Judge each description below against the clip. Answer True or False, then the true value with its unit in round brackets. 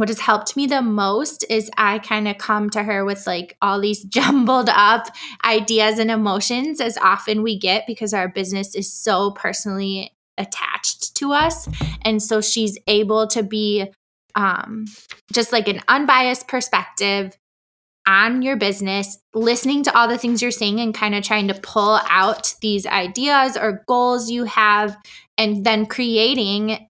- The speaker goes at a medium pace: True (165 wpm)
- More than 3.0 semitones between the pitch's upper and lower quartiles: False (2.7 semitones)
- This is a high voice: True (215 Hz)